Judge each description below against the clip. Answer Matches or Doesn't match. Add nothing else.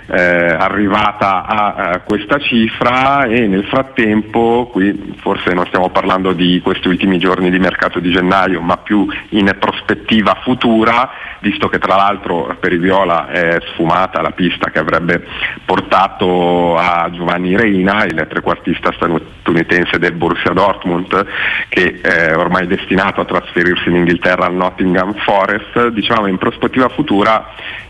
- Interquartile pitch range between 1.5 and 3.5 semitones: Matches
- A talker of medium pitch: Doesn't match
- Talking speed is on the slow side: Doesn't match